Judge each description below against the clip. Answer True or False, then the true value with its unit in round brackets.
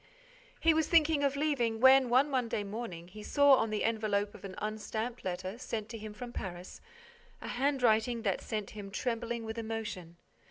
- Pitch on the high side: True (225 Hz)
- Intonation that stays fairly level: False (3.3 semitones)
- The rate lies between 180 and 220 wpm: True (185 wpm)